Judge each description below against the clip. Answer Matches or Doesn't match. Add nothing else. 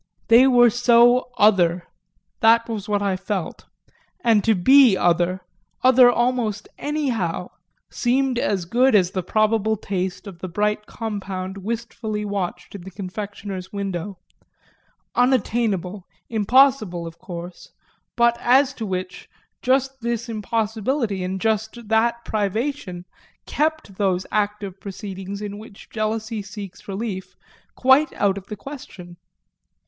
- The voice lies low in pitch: Doesn't match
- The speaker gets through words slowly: Matches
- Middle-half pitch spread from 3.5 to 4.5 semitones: Matches